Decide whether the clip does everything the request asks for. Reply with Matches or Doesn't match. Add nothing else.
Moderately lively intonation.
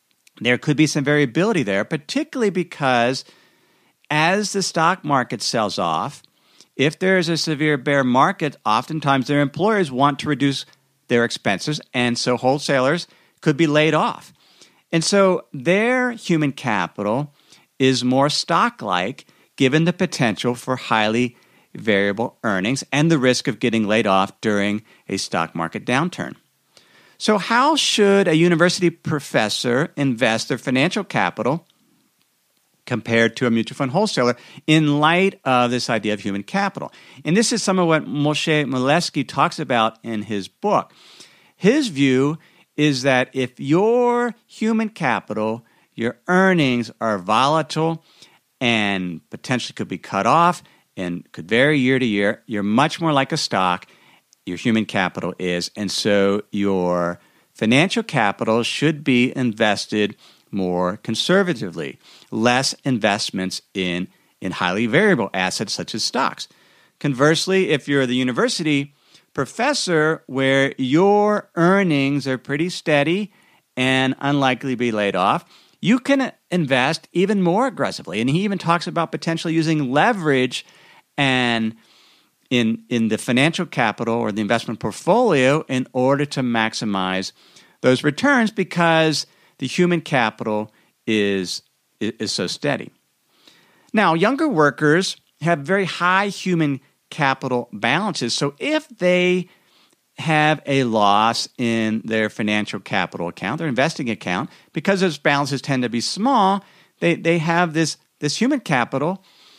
Doesn't match